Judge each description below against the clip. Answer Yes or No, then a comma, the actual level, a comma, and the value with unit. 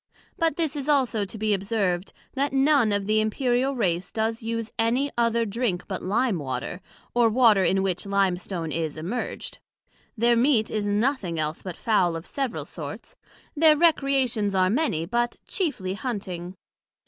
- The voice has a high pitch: Yes, high, 220 Hz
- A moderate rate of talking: Yes, average, 160 wpm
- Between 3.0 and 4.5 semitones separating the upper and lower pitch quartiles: No, average, 5.3 semitones